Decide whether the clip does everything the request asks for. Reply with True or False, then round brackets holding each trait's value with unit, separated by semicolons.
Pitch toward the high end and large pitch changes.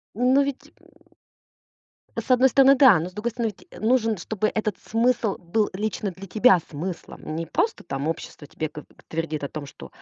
True (210 Hz; 6.6 semitones)